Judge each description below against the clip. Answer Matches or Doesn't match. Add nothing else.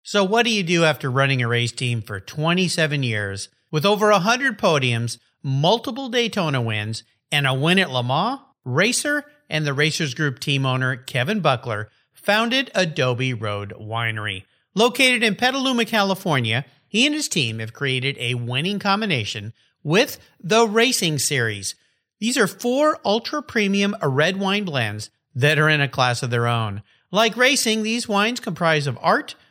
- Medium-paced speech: Matches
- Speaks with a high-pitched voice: Doesn't match